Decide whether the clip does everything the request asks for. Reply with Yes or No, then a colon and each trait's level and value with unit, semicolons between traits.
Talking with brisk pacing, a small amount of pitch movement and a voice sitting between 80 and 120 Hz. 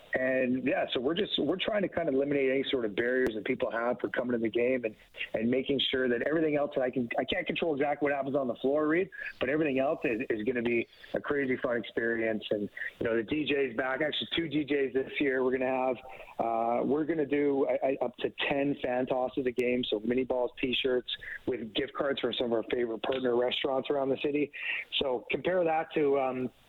No: fast, 240 wpm; narrow, 2.3 semitones; low, 130 Hz